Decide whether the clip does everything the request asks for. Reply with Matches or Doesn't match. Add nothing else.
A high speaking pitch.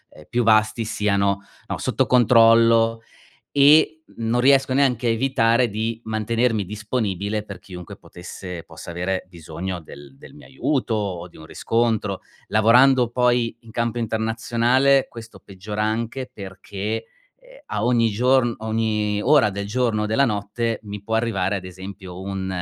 Doesn't match